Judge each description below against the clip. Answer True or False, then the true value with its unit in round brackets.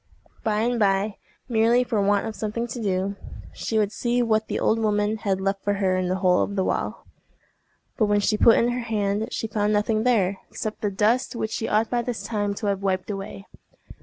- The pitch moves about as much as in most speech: False (2.1 semitones)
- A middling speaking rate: False (220 wpm)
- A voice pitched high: True (210 Hz)